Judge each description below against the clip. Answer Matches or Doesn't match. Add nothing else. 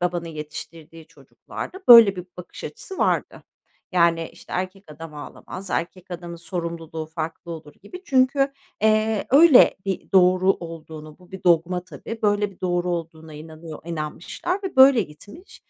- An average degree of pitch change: Matches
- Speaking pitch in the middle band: Matches